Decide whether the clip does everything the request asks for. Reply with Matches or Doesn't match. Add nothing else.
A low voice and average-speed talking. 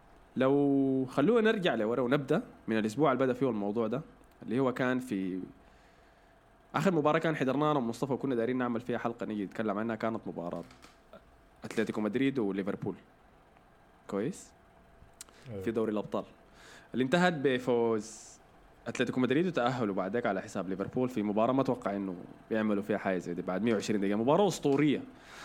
Doesn't match